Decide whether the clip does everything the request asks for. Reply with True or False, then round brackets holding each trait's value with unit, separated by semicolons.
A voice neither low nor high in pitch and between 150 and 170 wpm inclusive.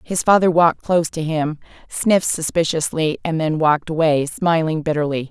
True (160 Hz; 160 wpm)